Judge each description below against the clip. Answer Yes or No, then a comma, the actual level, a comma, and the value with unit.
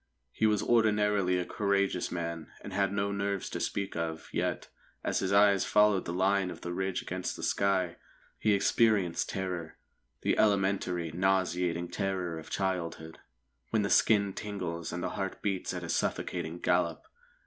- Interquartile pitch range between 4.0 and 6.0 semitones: No, narrow, 2.4 semitones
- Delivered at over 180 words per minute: No, average, 160 wpm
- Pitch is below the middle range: Yes, very low, 95 Hz